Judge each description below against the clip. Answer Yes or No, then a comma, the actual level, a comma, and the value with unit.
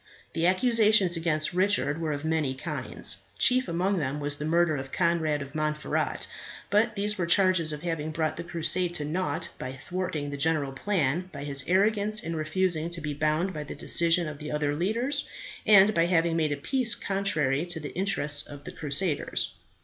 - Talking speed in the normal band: Yes, average, 190 wpm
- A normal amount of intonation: Yes, average, 3.8 semitones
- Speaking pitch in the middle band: Yes, medium, 165 Hz